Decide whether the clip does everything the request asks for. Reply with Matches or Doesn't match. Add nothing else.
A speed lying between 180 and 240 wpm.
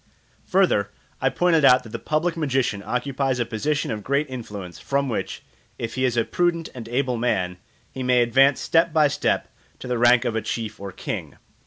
Matches